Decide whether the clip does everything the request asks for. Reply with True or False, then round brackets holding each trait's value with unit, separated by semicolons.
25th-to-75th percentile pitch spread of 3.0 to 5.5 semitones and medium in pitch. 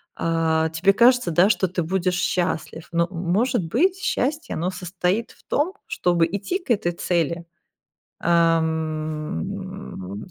True (3.4 semitones; 180 Hz)